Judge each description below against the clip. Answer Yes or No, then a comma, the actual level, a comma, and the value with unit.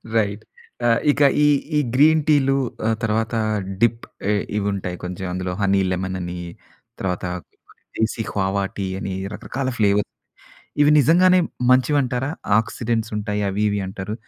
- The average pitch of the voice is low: Yes, low, 110 Hz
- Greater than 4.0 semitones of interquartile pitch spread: Yes, average, 4.7 semitones